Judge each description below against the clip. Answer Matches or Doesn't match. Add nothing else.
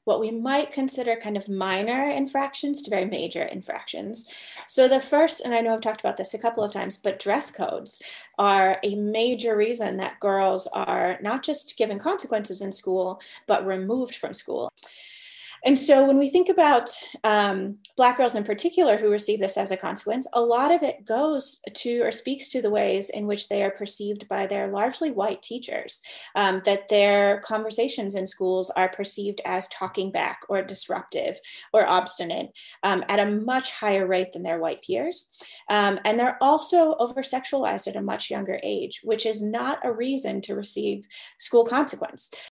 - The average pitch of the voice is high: Matches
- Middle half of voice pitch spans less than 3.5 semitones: Doesn't match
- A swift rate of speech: Doesn't match